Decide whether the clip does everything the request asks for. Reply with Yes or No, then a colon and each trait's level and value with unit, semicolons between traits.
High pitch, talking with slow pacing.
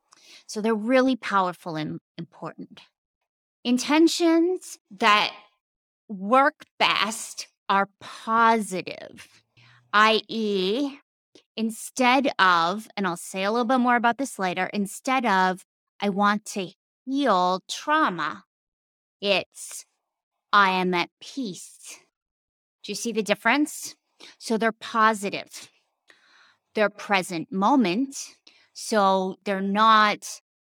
Yes: high, 210 Hz; slow, 100 wpm